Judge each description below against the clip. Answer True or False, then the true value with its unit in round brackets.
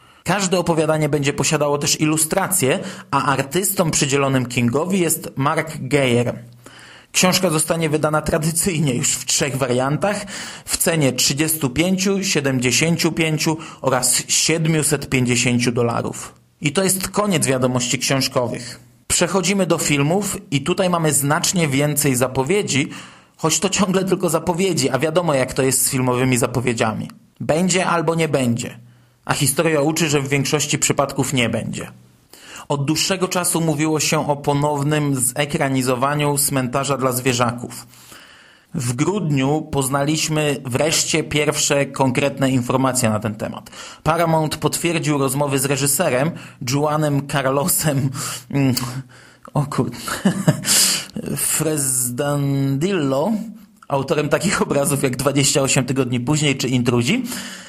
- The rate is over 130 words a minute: False (110 wpm)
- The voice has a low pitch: False (145 Hz)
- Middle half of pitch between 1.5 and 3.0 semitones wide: False (3.7 semitones)